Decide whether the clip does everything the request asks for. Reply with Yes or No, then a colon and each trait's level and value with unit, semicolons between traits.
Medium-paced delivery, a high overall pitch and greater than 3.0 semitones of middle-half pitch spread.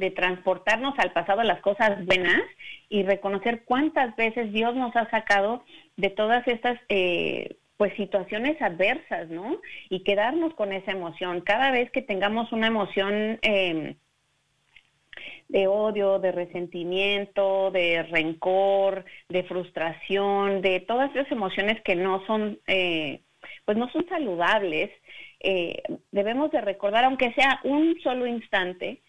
Yes: average, 135 wpm; high, 200 Hz; average, 3.9 semitones